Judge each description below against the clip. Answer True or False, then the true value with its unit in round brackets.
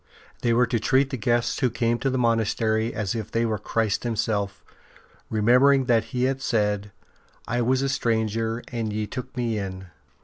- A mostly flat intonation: True (2.3 semitones)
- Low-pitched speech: True (115 Hz)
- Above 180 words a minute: True (190 wpm)